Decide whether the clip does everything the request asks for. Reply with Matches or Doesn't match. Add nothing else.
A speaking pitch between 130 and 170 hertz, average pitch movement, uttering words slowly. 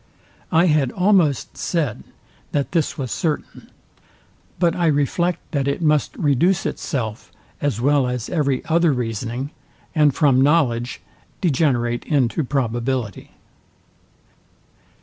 Matches